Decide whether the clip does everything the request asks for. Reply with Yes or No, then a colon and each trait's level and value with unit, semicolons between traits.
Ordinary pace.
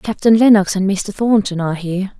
Yes: average, 190 wpm